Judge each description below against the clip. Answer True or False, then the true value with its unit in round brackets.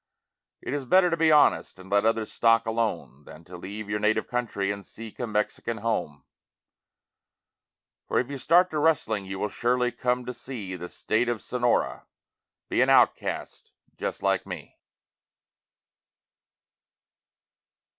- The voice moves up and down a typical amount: True (3.6 semitones)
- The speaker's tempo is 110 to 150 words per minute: True (145 wpm)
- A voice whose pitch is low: True (115 Hz)